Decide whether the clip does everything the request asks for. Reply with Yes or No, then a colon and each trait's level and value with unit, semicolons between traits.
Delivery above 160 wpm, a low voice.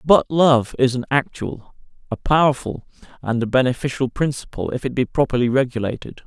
No: average, 155 wpm; low, 130 Hz